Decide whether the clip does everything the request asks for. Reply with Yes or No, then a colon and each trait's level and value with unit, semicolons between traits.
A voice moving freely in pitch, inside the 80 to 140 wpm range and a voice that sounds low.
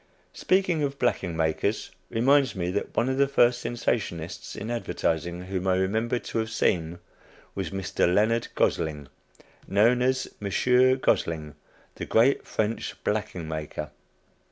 Yes: wide, 6.1 semitones; slow, 135 wpm; low, 105 Hz